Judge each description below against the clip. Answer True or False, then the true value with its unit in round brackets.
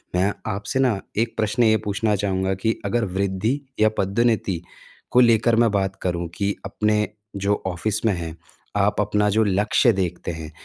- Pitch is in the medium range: False (105 Hz)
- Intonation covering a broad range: False (2.7 semitones)